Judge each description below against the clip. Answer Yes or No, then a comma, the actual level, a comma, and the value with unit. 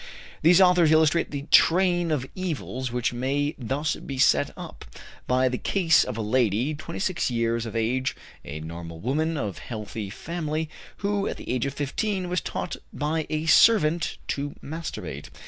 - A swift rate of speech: No, average, 165 wpm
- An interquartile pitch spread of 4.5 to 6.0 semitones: Yes, wide, 5.5 semitones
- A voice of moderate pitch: Yes, medium, 145 Hz